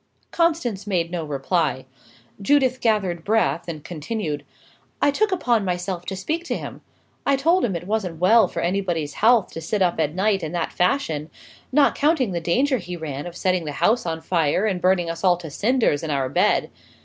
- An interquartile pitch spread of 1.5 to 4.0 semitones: No, wide, 5.5 semitones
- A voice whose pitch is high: No, medium, 180 Hz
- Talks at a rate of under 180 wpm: No, average, 195 wpm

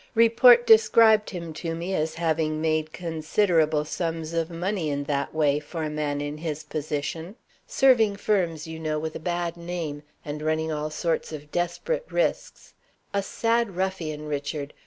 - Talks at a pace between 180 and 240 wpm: No, average, 160 wpm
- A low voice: No, medium, 160 Hz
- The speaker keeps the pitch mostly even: No, average, 3.4 semitones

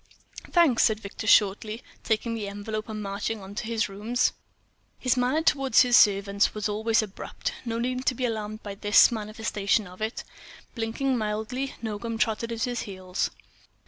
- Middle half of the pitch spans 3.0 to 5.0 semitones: No, narrow, 2.4 semitones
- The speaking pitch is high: Yes, high, 220 Hz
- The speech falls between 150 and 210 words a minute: Yes, average, 165 wpm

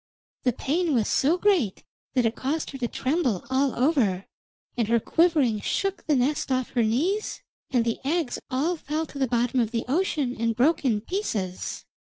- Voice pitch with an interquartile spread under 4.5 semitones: No, average, 5.2 semitones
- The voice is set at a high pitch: Yes, very high, 260 Hz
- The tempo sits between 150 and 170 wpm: No, average, 185 wpm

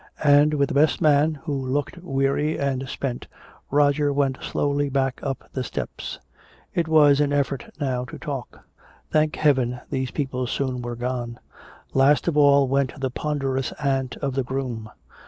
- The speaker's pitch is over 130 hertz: Yes, medium, 140 Hz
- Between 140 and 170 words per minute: Yes, average, 160 wpm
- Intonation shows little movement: Yes, narrow, 1.9 semitones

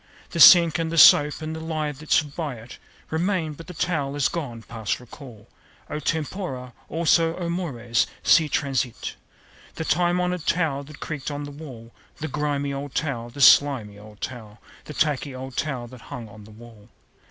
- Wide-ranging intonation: No, average, 4.6 semitones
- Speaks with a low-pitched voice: No, medium, 145 Hz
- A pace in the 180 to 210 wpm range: Yes, average, 185 wpm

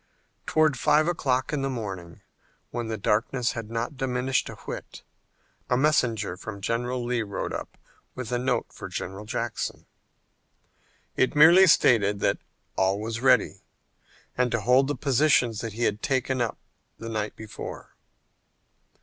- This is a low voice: Yes, low, 120 Hz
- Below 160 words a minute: Yes, average, 150 wpm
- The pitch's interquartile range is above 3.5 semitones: No, average, 3.2 semitones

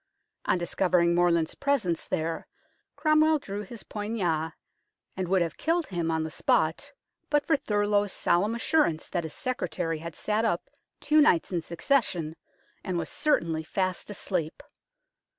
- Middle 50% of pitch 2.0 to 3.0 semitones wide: No, wide, 5.6 semitones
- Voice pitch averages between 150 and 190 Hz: Yes, medium, 185 Hz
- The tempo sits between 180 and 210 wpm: No, average, 145 wpm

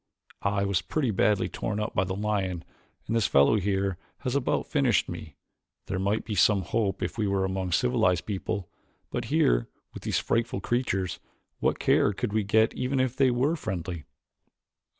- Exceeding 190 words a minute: No, average, 175 wpm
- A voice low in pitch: Yes, low, 100 Hz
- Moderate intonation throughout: Yes, average, 3.6 semitones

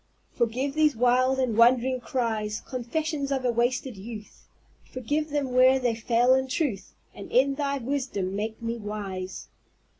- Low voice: No, very high, 250 Hz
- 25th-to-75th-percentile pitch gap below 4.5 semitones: Yes, average, 3.0 semitones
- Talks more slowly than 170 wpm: Yes, average, 150 wpm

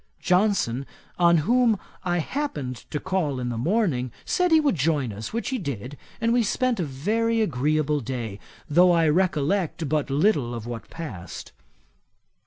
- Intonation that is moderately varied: No, wide, 7.8 semitones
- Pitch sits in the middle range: Yes, medium, 160 Hz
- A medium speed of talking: Yes, average, 160 wpm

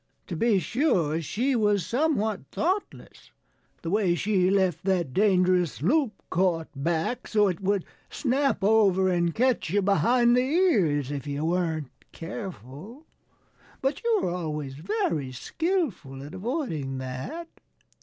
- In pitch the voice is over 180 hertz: Yes, high, 190 Hz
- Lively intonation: Yes, wide, 6.8 semitones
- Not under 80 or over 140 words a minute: Yes, slow, 135 wpm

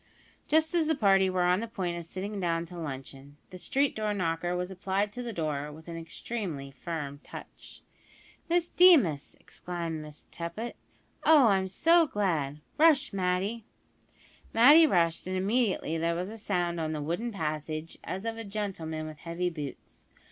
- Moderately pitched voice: Yes, medium, 180 Hz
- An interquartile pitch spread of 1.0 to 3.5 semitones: No, average, 5.1 semitones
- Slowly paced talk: No, average, 170 wpm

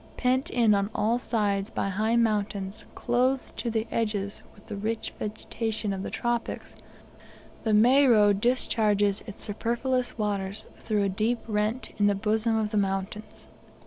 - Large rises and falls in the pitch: No, narrow, 2.4 semitones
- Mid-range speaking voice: No, high, 215 Hz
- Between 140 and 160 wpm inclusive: Yes, average, 150 wpm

